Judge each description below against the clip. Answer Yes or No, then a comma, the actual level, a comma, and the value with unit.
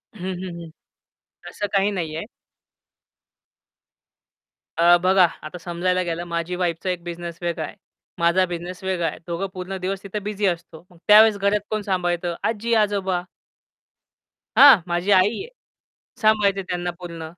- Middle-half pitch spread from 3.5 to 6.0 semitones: No, narrow, 2.5 semitones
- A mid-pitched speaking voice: Yes, medium, 180 Hz